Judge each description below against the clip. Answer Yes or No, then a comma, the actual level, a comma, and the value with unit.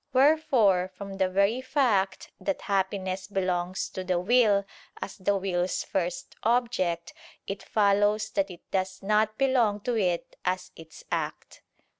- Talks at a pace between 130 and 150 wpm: Yes, average, 140 wpm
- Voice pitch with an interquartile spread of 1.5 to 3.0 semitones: Yes, average, 2.7 semitones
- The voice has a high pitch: Yes, high, 195 Hz